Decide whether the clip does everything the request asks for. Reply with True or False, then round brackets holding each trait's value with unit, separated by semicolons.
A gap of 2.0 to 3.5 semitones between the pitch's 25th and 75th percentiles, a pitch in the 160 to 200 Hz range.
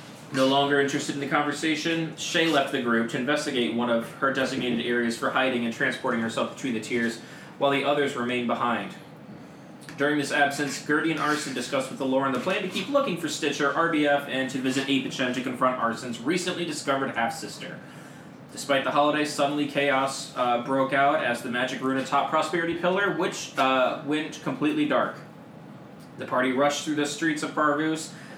False (2.6 semitones; 140 Hz)